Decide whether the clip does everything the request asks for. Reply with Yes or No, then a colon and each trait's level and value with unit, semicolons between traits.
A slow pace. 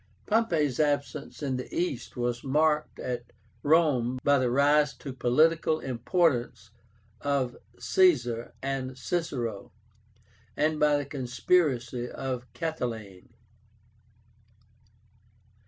Yes: slow, 95 wpm